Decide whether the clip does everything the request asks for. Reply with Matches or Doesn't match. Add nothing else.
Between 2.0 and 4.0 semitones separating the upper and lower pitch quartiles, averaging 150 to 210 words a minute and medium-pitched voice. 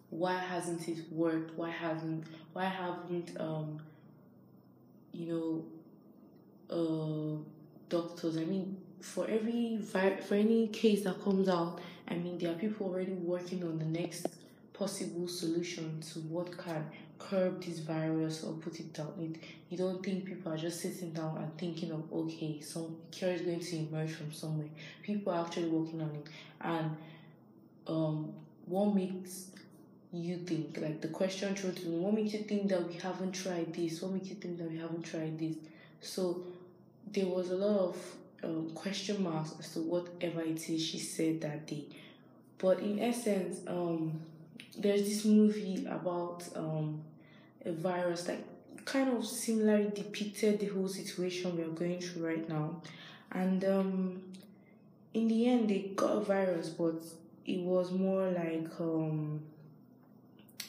Matches